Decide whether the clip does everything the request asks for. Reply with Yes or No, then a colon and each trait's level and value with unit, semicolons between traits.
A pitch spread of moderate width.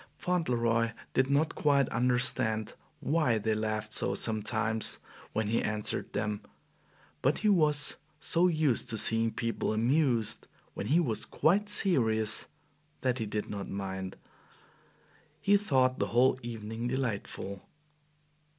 Yes: average, 4.4 semitones